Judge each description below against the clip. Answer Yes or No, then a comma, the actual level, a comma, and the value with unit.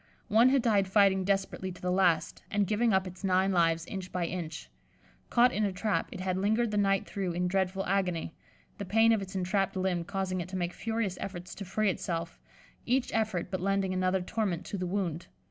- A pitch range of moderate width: No, narrow, 2.1 semitones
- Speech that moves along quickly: Yes, fast, 210 wpm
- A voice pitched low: No, high, 190 Hz